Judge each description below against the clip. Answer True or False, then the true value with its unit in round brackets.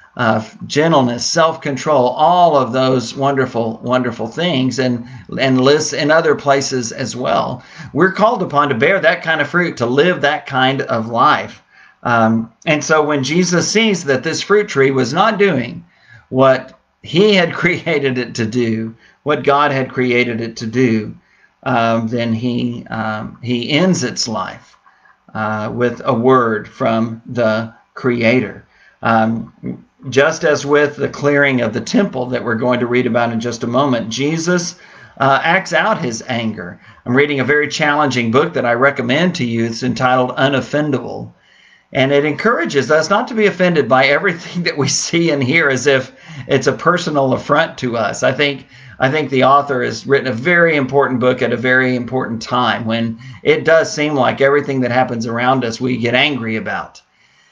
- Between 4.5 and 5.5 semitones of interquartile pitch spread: False (3.7 semitones)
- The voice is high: False (130 Hz)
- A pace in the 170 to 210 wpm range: True (175 wpm)